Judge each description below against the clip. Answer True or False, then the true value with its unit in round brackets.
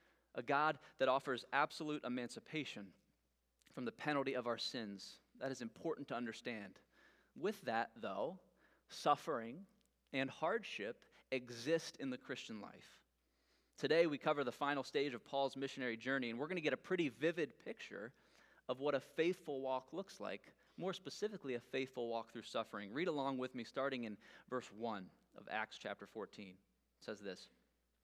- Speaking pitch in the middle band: False (130 Hz)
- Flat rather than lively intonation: False (4.1 semitones)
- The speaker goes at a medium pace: True (165 wpm)